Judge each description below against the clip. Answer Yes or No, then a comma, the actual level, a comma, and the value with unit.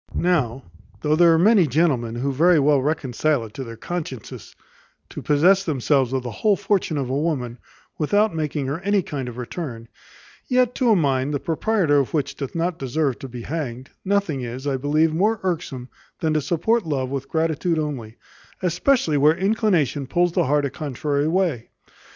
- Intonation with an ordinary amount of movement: Yes, average, 4.8 semitones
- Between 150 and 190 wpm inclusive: Yes, average, 180 wpm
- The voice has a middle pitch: Yes, medium, 150 Hz